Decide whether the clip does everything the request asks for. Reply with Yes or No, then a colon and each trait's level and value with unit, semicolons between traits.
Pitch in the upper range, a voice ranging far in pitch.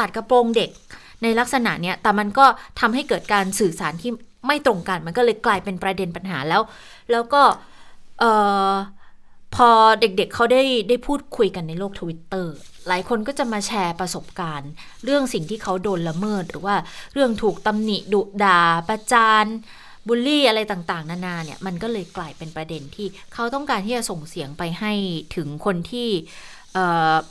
No: high, 200 Hz; average, 4.6 semitones